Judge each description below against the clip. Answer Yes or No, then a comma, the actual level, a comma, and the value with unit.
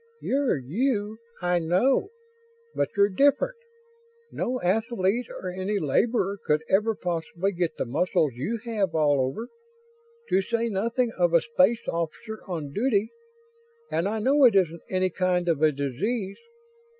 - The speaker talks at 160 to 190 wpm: No, average, 145 wpm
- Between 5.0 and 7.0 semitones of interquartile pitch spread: Yes, average, 5.3 semitones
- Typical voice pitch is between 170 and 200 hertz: Yes, high, 190 Hz